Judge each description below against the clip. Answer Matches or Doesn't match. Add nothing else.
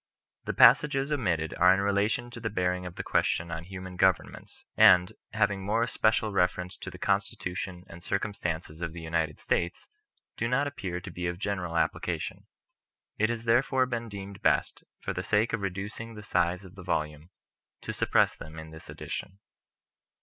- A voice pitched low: Matches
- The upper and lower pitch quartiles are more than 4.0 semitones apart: Doesn't match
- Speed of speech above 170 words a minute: Matches